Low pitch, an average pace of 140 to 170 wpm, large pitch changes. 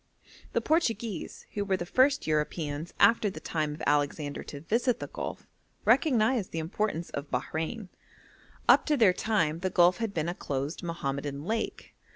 No: medium, 175 Hz; average, 165 wpm; wide, 6.6 semitones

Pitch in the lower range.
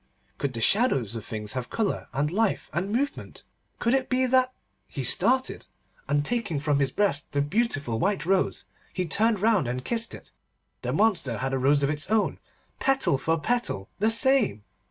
No: medium, 185 Hz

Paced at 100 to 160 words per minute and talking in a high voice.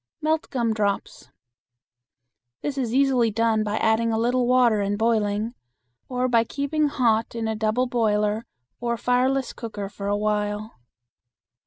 Yes: average, 145 wpm; high, 230 Hz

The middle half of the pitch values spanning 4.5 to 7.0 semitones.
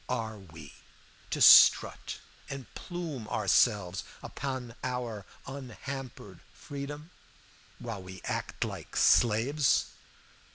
Yes: average, 4.9 semitones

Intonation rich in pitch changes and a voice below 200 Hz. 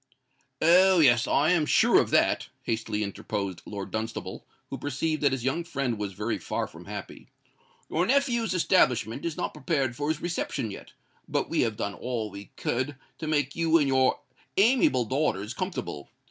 Yes: wide, 6.7 semitones; low, 135 Hz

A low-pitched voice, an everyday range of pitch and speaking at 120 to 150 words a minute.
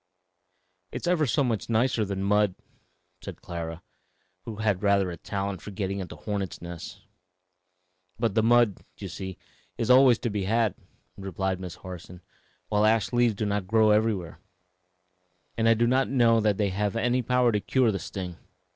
No: low, 105 Hz; average, 3.2 semitones; average, 170 wpm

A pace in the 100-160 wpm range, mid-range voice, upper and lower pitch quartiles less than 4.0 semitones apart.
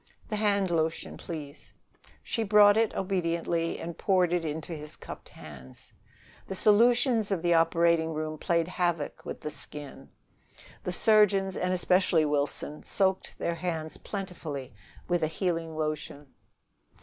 Yes: slow, 135 wpm; medium, 170 Hz; average, 3.5 semitones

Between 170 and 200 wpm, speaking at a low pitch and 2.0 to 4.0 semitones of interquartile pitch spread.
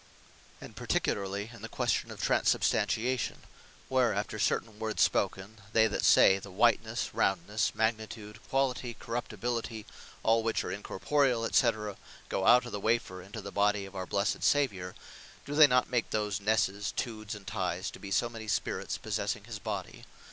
Yes: average, 175 wpm; low, 110 Hz; average, 2.8 semitones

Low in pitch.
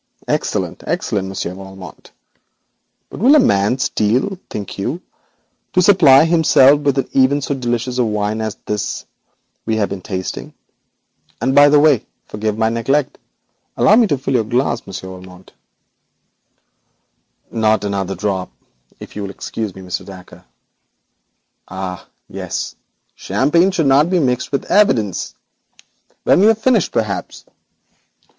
Yes: low, 115 Hz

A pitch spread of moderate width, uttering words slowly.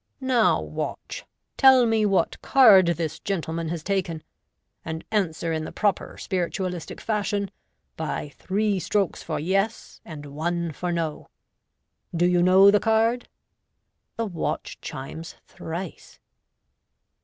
Yes: average, 4.0 semitones; slow, 125 wpm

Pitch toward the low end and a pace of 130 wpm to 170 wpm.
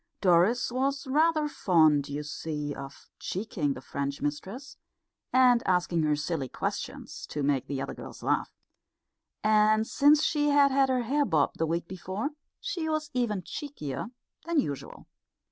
No: high, 200 Hz; average, 150 wpm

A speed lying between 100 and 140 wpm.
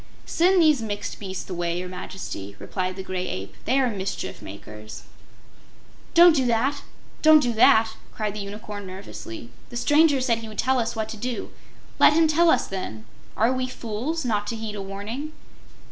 No: average, 180 wpm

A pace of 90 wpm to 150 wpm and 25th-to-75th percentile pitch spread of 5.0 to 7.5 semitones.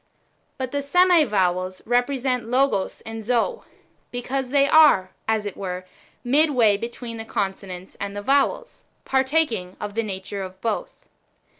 Yes: average, 145 wpm; wide, 5.5 semitones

